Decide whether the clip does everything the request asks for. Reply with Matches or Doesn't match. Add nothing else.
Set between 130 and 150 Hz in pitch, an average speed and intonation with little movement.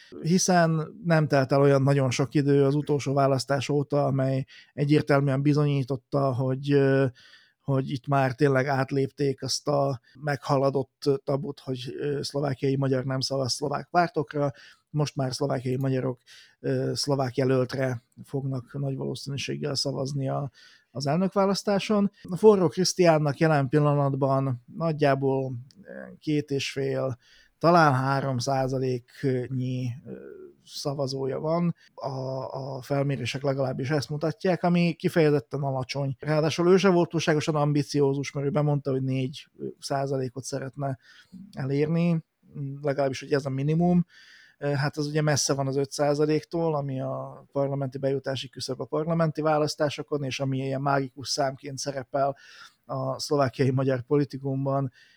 Matches